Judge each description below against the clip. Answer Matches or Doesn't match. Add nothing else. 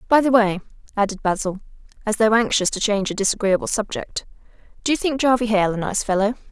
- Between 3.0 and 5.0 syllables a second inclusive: Doesn't match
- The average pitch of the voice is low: Doesn't match